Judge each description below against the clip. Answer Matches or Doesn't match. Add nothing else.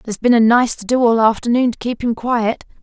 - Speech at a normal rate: Doesn't match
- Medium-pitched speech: Doesn't match